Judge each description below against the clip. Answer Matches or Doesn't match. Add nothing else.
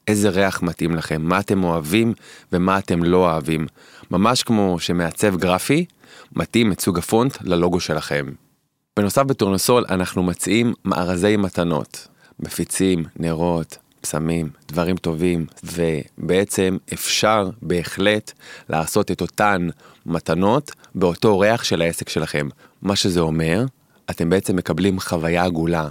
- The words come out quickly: Doesn't match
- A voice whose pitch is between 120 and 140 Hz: Doesn't match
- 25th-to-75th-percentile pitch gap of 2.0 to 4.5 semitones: Matches